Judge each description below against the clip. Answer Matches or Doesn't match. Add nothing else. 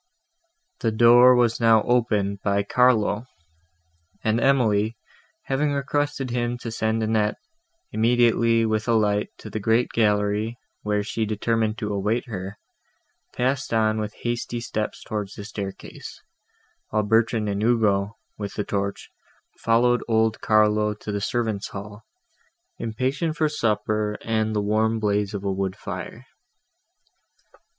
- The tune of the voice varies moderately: Doesn't match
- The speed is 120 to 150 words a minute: Matches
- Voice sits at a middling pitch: Doesn't match